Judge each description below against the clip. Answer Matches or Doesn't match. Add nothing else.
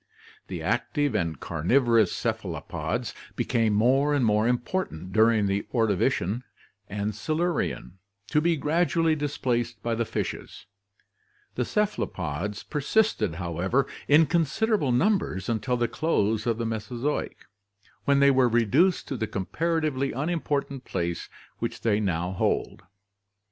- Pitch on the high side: Doesn't match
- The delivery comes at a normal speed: Doesn't match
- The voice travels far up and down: Matches